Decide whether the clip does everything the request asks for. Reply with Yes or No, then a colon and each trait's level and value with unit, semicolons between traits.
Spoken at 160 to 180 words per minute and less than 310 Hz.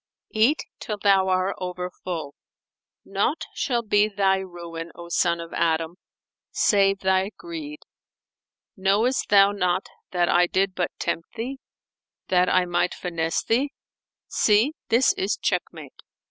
No: average, 140 wpm; high, 190 Hz